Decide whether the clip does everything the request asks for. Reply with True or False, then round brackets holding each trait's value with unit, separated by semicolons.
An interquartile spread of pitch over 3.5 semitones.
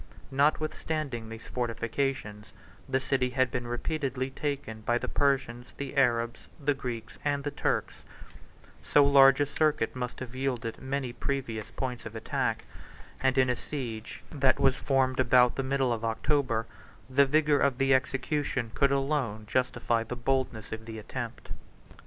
False (2.7 semitones)